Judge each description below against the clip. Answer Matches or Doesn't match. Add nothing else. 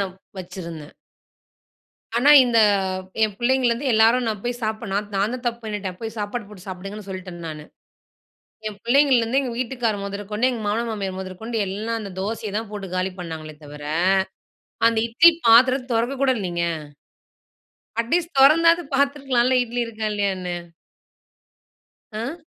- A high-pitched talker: Matches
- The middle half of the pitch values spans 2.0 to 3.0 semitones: Doesn't match